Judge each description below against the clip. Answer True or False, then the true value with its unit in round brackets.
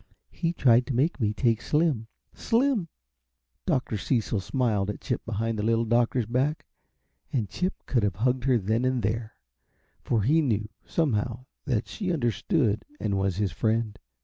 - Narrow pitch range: False (3.9 semitones)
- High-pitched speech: False (120 Hz)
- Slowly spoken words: False (160 wpm)